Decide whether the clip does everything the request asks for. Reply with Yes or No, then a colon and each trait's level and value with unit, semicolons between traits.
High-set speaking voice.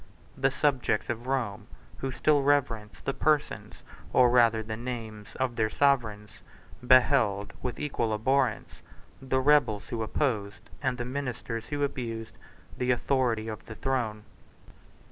No: low, 125 Hz